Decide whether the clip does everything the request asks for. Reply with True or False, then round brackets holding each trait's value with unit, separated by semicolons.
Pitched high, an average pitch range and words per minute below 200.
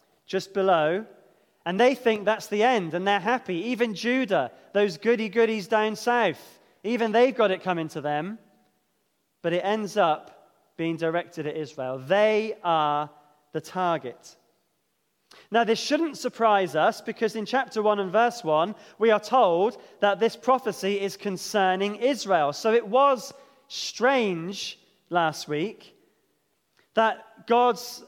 True (210 Hz; 4.8 semitones; 140 wpm)